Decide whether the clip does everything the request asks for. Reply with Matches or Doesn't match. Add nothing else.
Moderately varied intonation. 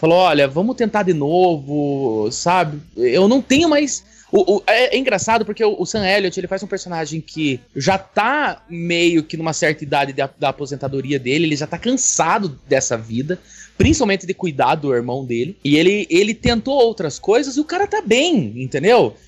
Doesn't match